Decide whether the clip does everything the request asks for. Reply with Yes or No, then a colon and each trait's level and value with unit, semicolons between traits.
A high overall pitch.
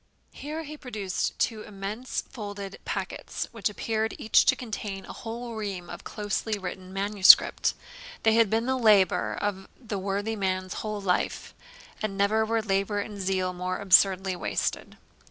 Yes: high, 205 Hz